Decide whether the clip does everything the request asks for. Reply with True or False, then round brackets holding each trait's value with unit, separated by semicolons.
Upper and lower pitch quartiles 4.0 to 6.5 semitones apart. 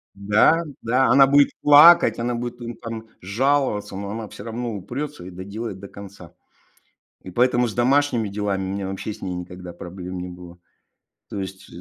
True (4.5 semitones)